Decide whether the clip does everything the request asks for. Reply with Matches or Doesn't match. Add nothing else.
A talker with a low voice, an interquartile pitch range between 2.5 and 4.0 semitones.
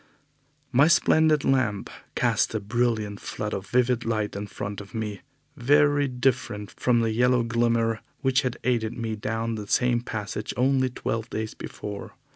Matches